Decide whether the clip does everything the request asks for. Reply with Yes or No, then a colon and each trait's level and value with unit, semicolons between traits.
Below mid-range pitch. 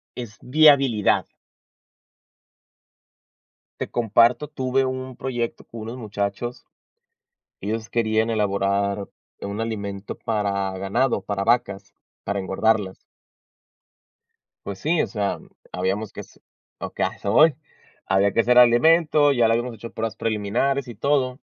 Yes: low, 115 Hz